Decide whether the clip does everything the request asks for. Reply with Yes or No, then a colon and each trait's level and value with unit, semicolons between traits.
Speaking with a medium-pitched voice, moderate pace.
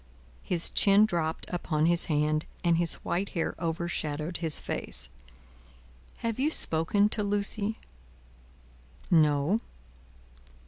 No: medium, 170 Hz; slow, 105 wpm